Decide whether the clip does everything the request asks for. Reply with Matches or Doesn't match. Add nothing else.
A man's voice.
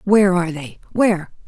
Doesn't match